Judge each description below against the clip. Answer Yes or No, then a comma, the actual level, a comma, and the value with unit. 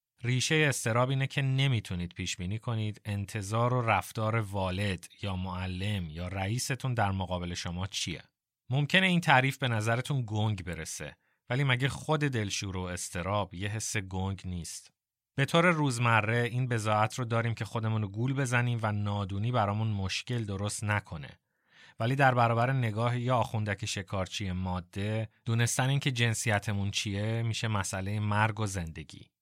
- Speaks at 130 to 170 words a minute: Yes, average, 150 wpm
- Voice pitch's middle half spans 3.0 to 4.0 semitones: Yes, average, 3.7 semitones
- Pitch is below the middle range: Yes, low, 110 Hz